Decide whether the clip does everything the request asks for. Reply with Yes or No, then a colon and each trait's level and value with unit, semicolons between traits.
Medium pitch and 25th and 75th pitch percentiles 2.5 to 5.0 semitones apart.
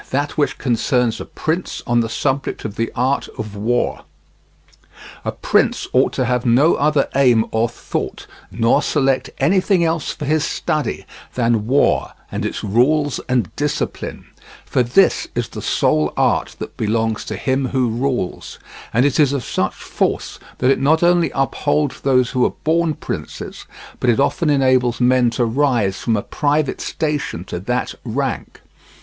No: low, 130 Hz; average, 3.7 semitones